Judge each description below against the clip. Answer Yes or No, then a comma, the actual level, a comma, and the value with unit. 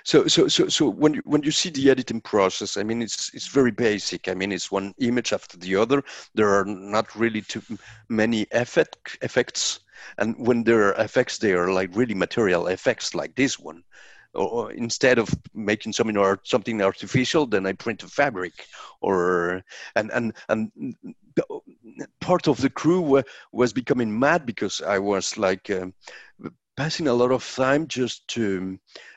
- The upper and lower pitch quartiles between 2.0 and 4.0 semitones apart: No, wide, 5.6 semitones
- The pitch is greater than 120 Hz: No, low, 115 Hz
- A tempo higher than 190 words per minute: No, average, 175 wpm